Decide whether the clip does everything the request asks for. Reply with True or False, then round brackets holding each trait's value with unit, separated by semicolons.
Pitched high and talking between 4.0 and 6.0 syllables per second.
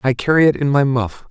False (130 Hz; 5.9 syllables/s)